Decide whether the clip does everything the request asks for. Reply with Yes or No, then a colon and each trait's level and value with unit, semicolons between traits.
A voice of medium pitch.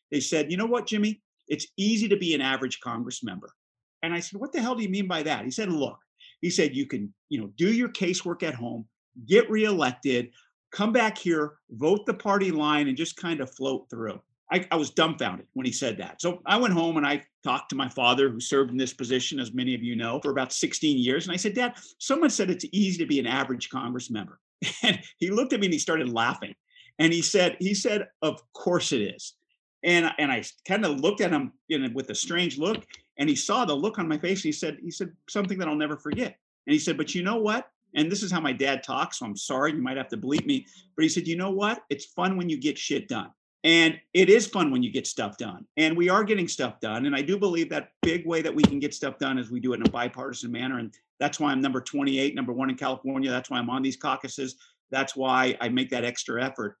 Yes: medium, 165 Hz